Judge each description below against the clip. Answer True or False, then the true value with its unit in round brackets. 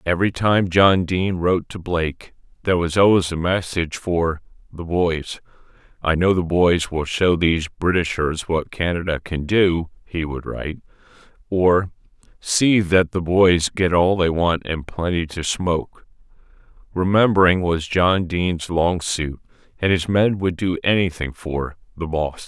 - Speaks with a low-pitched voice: True (85 Hz)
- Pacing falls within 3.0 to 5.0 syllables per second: True (4.5 syllables/s)